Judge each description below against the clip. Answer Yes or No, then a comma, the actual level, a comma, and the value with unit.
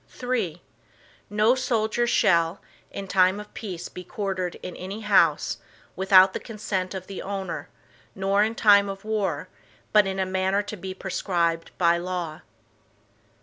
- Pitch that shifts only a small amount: Yes, narrow, 2.3 semitones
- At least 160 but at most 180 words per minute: No, average, 150 wpm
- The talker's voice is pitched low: No, high, 190 Hz